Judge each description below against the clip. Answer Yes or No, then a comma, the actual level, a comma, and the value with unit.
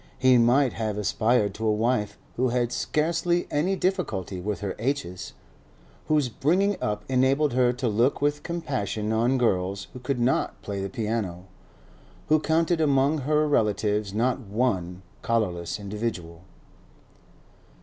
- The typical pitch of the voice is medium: No, low, 120 Hz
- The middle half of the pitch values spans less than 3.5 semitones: No, wide, 5.5 semitones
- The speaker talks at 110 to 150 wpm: Yes, average, 140 wpm